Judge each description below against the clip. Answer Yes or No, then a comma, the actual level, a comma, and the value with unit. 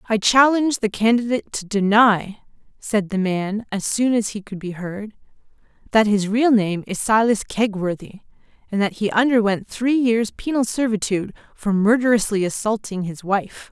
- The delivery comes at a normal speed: Yes, average, 155 wpm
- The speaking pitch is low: No, high, 215 Hz